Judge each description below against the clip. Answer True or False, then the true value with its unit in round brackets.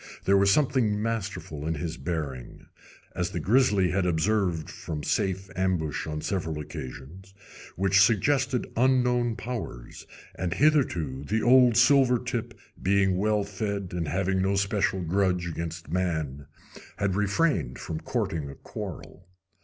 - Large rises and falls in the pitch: False (5.0 semitones)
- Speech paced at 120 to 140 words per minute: True (135 wpm)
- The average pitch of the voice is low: True (95 Hz)